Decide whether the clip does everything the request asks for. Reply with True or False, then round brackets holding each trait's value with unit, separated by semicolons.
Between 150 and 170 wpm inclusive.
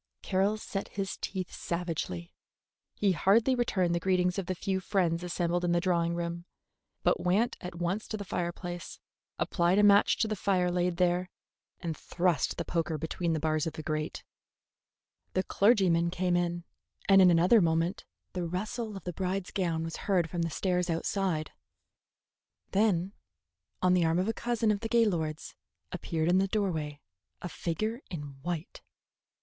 True (165 wpm)